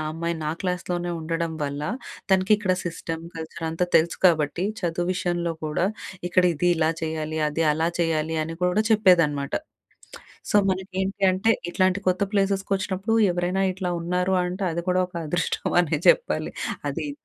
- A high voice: No, medium, 175 Hz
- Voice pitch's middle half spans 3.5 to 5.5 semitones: No, narrow, 2.5 semitones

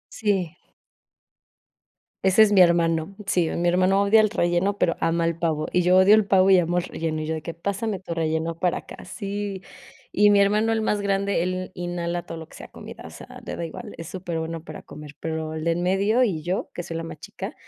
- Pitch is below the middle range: No, medium, 180 Hz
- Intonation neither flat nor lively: Yes, average, 3.1 semitones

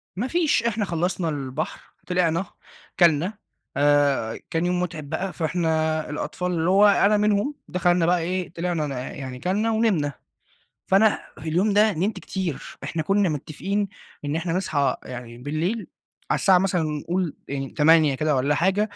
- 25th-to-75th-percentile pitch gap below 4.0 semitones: No, average, 4.3 semitones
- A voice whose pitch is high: No, medium, 175 Hz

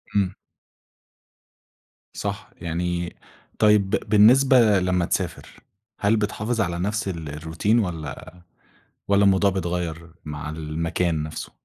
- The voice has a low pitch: Yes, very low, 90 Hz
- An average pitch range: Yes, average, 3.9 semitones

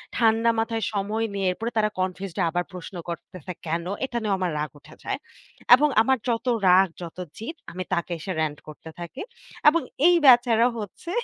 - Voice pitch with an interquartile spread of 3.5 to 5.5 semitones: Yes, average, 4.6 semitones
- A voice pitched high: Yes, high, 200 Hz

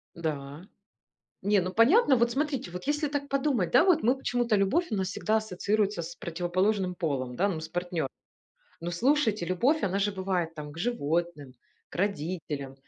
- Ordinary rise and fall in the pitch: No, wide, 5.9 semitones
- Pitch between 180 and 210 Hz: Yes, high, 190 Hz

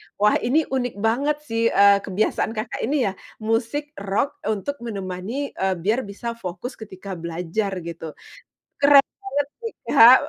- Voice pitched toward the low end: No, high, 225 Hz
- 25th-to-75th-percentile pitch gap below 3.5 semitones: No, average, 5.2 semitones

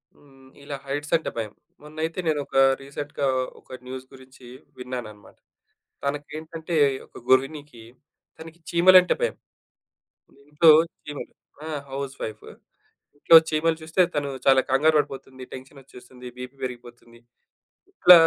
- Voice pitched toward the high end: No, medium, 140 Hz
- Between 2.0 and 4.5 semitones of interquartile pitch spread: Yes, average, 3.3 semitones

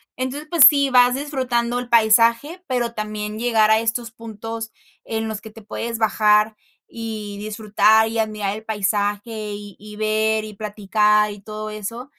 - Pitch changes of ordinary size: No, narrow, 1.7 semitones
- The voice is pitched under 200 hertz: No, high, 220 Hz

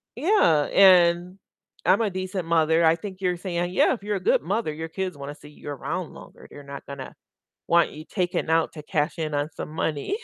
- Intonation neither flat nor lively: Yes, average, 3.6 semitones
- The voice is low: No, medium, 170 Hz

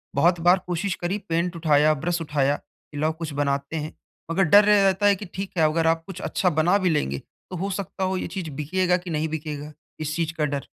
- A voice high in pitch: No, medium, 165 Hz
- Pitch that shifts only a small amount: No, average, 3.5 semitones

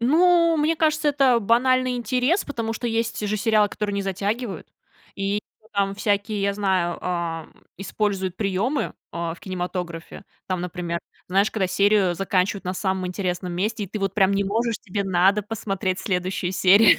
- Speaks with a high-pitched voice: Yes, high, 200 Hz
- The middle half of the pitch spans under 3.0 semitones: No, average, 3.4 semitones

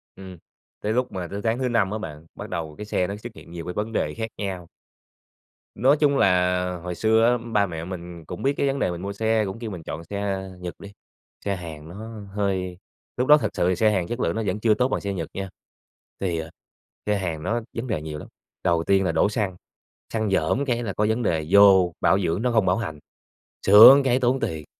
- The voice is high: No, low, 100 Hz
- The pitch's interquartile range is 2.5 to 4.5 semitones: Yes, average, 4.1 semitones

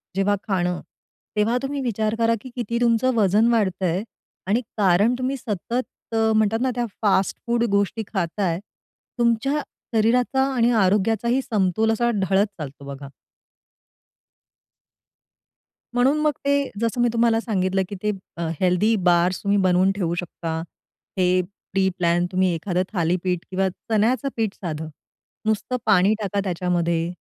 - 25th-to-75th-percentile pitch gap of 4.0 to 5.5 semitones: Yes, average, 4.3 semitones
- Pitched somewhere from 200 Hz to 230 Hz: Yes, high, 205 Hz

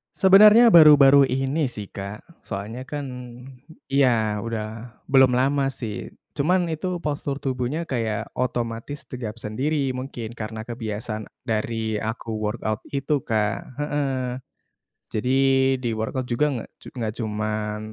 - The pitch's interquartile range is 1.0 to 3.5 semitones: No, average, 4.2 semitones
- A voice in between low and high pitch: No, low, 125 Hz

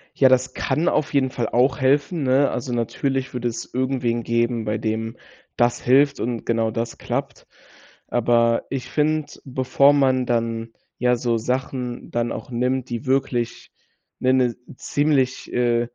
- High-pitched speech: No, low, 125 Hz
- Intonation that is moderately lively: No, narrow, 2.2 semitones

